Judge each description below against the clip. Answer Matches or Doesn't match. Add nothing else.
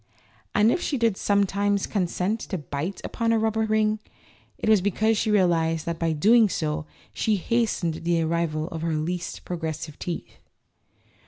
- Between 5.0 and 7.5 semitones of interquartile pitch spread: Doesn't match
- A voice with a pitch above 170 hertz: Matches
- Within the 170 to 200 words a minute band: Doesn't match